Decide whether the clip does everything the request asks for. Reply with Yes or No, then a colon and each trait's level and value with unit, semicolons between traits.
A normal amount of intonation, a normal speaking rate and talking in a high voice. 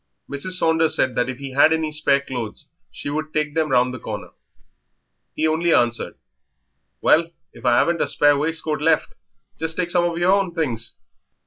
No: average, 3.5 semitones; average, 185 wpm; medium, 155 Hz